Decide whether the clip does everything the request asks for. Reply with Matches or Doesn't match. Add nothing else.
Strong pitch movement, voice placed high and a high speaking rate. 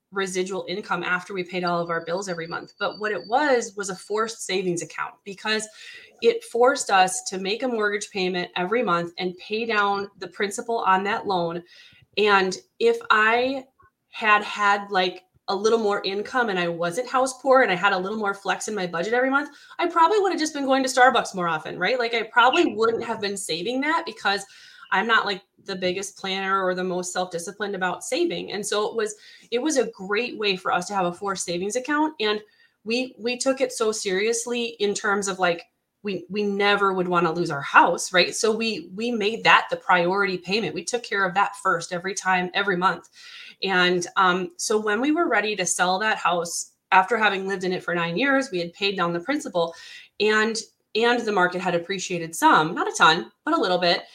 Doesn't match